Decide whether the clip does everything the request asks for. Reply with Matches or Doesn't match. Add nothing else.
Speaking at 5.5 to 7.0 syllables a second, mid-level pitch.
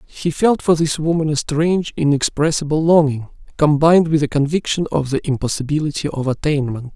Matches